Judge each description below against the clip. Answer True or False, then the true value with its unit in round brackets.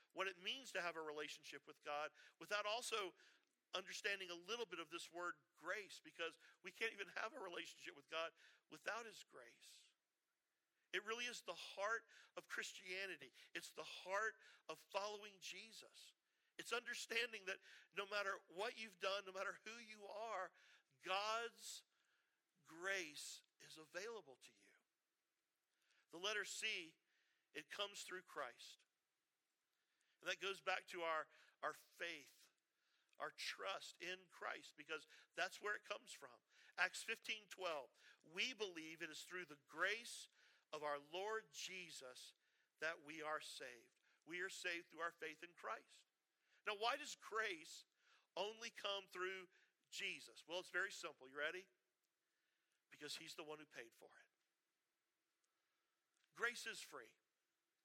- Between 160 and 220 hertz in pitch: True (190 Hz)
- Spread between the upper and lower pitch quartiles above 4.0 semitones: True (4.7 semitones)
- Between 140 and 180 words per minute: True (145 wpm)